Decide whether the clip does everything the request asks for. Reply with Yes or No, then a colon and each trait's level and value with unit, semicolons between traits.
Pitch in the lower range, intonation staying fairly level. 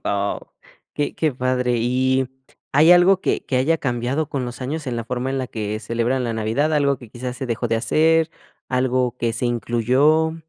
No: low, 130 Hz; average, 3.4 semitones